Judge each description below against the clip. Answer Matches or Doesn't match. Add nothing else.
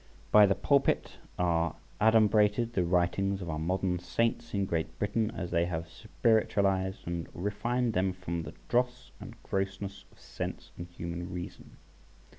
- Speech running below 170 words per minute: Matches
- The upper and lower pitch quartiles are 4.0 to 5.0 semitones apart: Doesn't match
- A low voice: Matches